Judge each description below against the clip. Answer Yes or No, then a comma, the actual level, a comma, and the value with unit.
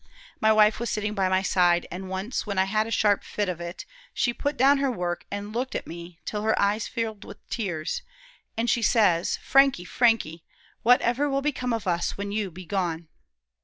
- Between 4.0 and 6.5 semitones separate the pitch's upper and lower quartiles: Yes, average, 4.3 semitones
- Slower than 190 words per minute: No, average, 200 wpm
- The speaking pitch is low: No, high, 210 Hz